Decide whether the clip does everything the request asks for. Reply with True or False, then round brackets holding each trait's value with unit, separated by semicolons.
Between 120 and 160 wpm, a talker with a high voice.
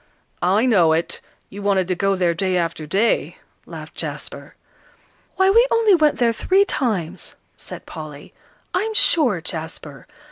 True (145 wpm; 195 Hz)